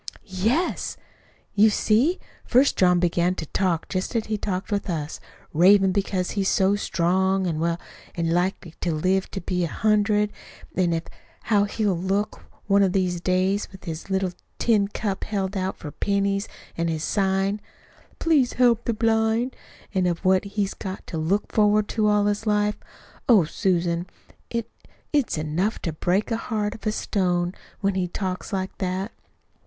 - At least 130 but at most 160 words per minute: No, average, 170 wpm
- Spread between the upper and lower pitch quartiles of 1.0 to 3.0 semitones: Yes, average, 2.7 semitones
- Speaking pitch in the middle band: No, high, 195 Hz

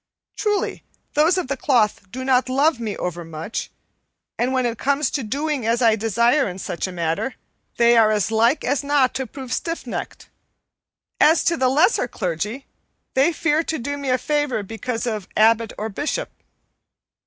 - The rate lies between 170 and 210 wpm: Yes, average, 175 wpm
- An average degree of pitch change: Yes, average, 4.6 semitones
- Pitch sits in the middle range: No, very high, 250 Hz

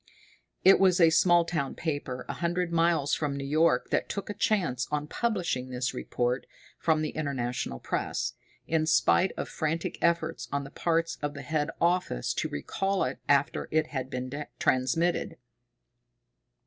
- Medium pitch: Yes, medium, 155 Hz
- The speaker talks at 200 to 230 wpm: No, average, 160 wpm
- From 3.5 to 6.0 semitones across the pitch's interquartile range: Yes, average, 3.9 semitones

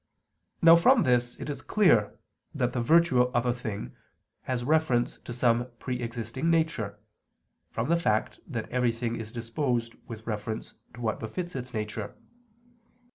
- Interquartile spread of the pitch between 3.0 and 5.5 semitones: Yes, average, 3.3 semitones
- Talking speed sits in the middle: Yes, average, 150 wpm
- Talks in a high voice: No, low, 120 Hz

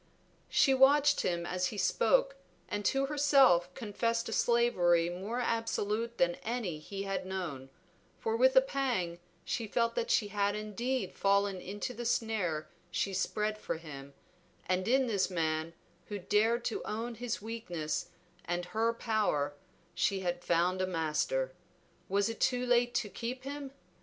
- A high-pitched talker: Yes, high, 210 Hz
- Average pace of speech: Yes, average, 155 wpm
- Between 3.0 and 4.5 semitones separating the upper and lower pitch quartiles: No, average, 5.1 semitones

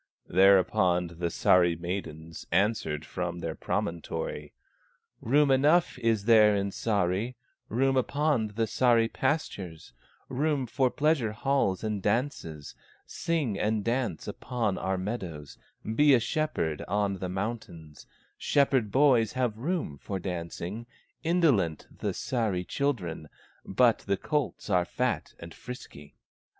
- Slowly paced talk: Yes, slow, 120 wpm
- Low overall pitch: Yes, low, 105 Hz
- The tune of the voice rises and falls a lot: Yes, wide, 6.3 semitones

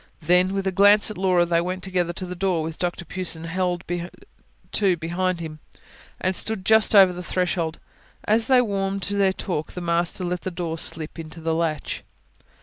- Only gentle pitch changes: Yes, narrow, 2.2 semitones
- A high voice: No, medium, 180 Hz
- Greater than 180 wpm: Yes, average, 190 wpm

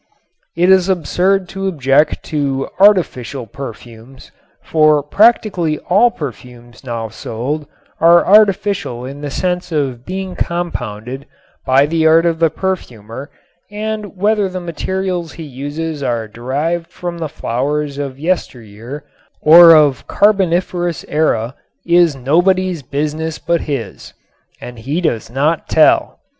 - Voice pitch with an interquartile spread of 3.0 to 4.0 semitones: No, average, 5.0 semitones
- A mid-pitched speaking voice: Yes, medium, 155 Hz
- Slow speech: Yes, slow, 125 wpm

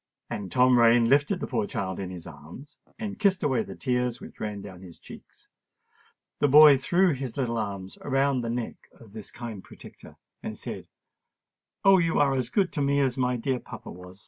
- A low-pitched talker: Yes, low, 125 Hz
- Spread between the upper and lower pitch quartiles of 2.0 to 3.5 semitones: No, average, 5.2 semitones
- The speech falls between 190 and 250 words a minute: Yes, average, 200 wpm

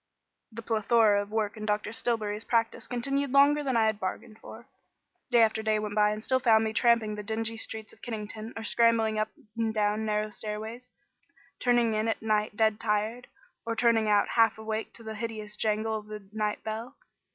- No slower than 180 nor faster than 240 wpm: Yes, average, 195 wpm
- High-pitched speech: Yes, high, 220 Hz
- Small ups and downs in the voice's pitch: Yes, narrow, 1.3 semitones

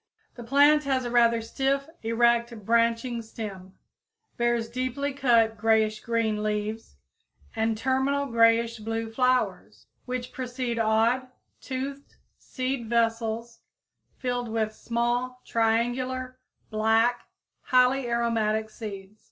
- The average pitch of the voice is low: No, high, 235 Hz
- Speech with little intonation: Yes, narrow, 2.1 semitones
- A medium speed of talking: No, slow, 105 wpm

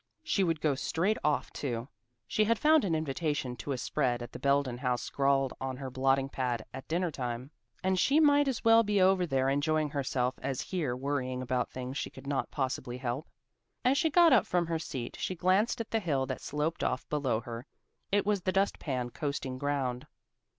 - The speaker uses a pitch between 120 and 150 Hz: Yes, medium, 140 Hz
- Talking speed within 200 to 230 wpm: Yes, fast, 205 wpm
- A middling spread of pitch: No, wide, 6.0 semitones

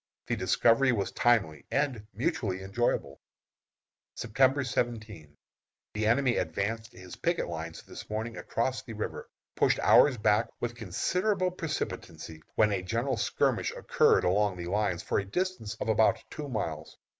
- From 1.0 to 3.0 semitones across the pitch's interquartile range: No, average, 4.9 semitones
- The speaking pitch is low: Yes, low, 110 Hz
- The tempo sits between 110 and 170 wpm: Yes, average, 145 wpm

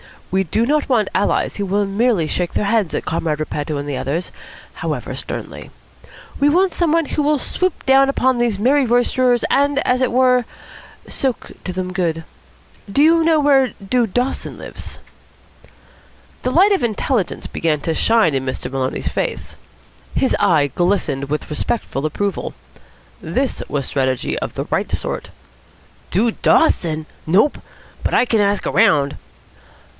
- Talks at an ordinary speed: Yes, average, 155 wpm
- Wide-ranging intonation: Yes, wide, 8.3 semitones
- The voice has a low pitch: No, high, 215 Hz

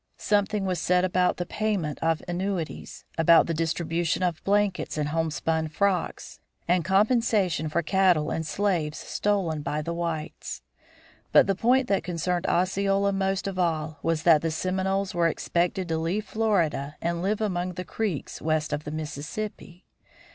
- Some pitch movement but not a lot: Yes, average, 3.4 semitones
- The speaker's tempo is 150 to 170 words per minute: Yes, average, 155 wpm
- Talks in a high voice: No, medium, 175 Hz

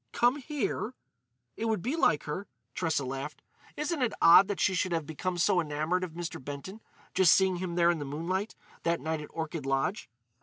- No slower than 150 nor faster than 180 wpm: No, average, 190 wpm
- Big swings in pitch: No, average, 4.3 semitones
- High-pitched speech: No, medium, 175 Hz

